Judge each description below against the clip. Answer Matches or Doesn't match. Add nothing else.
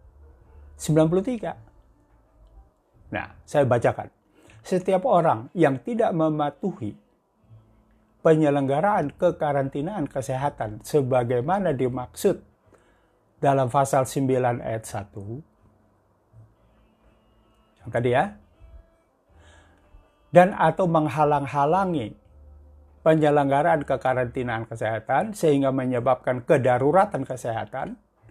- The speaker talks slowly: Matches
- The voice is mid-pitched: Doesn't match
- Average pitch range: Doesn't match